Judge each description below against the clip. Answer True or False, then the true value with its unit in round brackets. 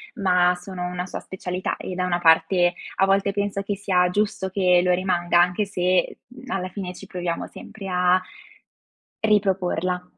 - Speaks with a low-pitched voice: False (185 Hz)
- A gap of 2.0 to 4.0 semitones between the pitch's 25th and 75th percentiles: False (1.6 semitones)